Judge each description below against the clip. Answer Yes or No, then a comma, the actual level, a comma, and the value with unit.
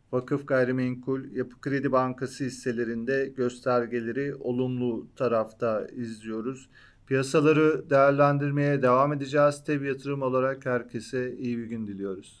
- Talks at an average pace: Yes, average, 105 wpm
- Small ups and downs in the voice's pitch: Yes, narrow, 2.2 semitones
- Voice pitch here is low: Yes, low, 130 Hz